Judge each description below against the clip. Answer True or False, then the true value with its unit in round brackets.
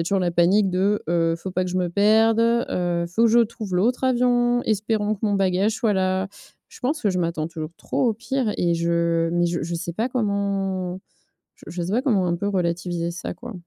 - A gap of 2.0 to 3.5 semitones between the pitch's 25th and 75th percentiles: False (4.3 semitones)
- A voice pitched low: False (190 Hz)